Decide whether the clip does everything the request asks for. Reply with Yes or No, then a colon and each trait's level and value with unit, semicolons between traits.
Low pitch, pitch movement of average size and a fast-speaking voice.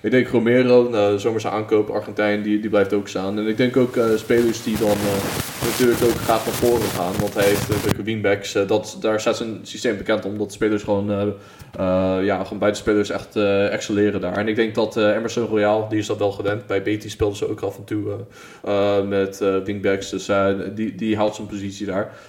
No: low, 105 Hz; narrow, 1.9 semitones; fast, 235 wpm